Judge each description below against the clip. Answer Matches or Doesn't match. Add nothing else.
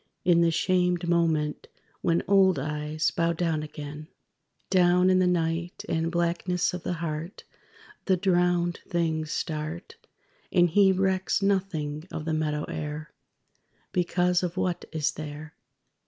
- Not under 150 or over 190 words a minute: Doesn't match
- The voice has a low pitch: Doesn't match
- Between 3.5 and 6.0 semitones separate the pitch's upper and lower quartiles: Doesn't match